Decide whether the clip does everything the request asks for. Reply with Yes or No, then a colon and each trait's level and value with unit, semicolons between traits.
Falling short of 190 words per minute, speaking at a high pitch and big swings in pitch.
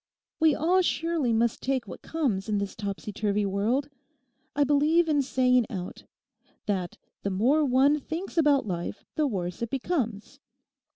Yes: average, 150 wpm; very high, 255 Hz; wide, 6.5 semitones